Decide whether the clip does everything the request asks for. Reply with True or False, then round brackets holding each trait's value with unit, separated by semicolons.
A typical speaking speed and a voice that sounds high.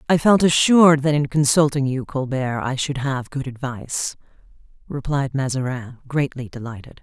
False (145 wpm; 135 Hz)